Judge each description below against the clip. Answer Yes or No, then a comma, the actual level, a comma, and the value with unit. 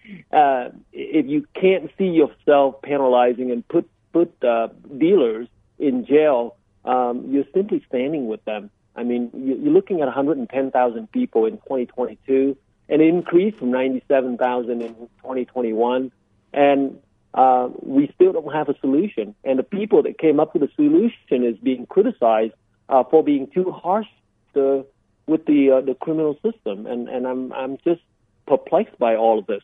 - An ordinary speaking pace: Yes, average, 155 wpm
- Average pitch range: No, wide, 5.9 semitones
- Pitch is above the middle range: No, low, 135 Hz